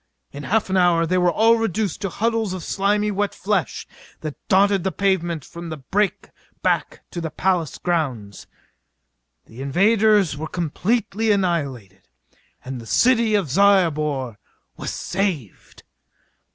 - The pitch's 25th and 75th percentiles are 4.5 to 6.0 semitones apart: Yes, average, 5.0 semitones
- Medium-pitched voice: Yes, medium, 180 Hz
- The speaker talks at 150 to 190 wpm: No, average, 140 wpm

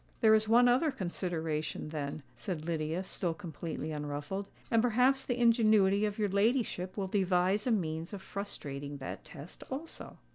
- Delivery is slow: No, average, 155 wpm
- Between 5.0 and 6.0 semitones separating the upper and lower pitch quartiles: Yes, wide, 5.5 semitones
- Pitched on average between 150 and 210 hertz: Yes, high, 190 Hz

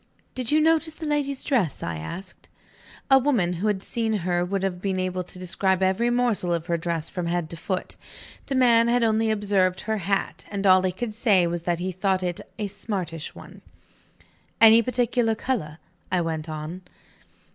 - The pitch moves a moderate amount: Yes, average, 4.6 semitones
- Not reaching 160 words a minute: No, average, 190 wpm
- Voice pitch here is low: No, high, 190 Hz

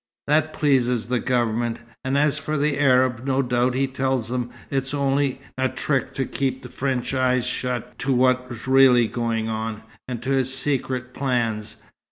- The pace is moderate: Yes, average, 165 wpm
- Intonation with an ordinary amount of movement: No, narrow, 1.8 semitones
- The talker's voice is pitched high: No, low, 130 Hz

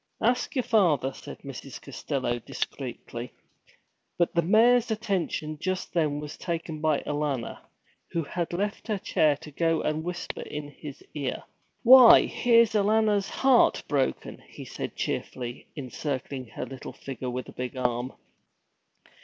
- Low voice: No, medium, 155 Hz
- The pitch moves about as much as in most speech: No, wide, 6.8 semitones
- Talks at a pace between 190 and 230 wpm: No, average, 140 wpm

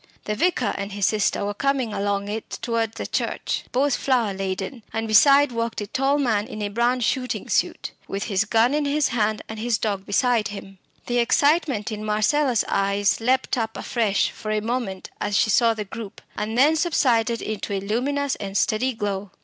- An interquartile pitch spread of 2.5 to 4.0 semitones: Yes, average, 3.6 semitones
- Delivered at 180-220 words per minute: Yes, average, 190 wpm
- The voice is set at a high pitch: Yes, high, 225 Hz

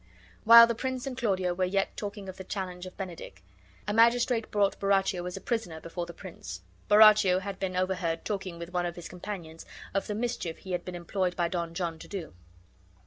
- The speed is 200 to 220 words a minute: Yes, fast, 205 wpm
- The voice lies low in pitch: No, medium, 185 Hz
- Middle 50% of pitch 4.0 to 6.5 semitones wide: No, average, 2.9 semitones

